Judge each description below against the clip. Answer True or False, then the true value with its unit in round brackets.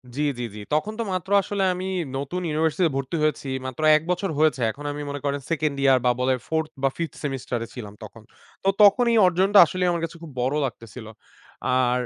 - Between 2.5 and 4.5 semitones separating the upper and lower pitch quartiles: False (5.3 semitones)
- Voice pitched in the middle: True (150 Hz)